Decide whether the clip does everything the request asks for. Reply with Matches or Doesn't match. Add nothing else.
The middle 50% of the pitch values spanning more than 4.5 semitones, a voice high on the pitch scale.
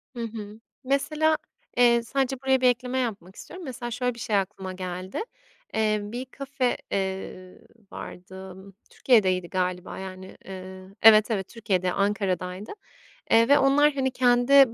Matches